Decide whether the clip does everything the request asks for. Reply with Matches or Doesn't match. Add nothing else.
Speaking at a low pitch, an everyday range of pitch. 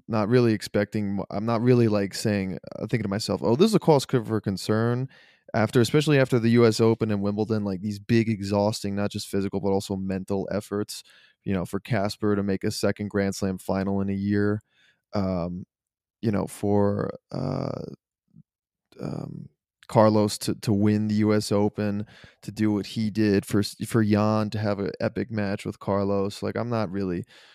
Doesn't match